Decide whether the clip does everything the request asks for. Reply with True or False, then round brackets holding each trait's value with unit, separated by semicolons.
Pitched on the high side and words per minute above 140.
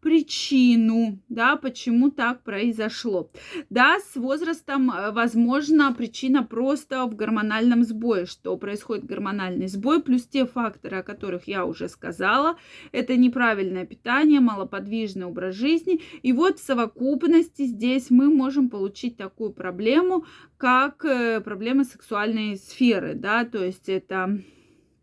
False (240 Hz; 120 wpm)